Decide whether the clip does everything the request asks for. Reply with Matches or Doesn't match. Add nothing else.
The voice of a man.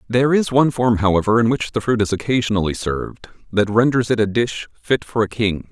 Matches